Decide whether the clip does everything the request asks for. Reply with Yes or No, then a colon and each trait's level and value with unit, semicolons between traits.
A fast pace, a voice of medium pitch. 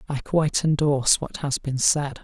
No: average, 190 wpm; medium, 145 Hz